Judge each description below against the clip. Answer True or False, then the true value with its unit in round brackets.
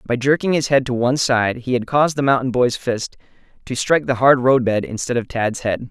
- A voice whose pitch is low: True (125 Hz)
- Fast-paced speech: True (235 wpm)